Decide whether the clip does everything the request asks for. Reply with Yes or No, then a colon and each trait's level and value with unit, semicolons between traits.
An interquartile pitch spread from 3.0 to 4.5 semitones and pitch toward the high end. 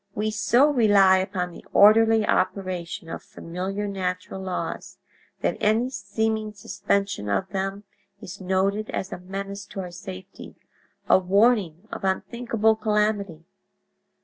No: narrow, 2.6 semitones; high, 195 Hz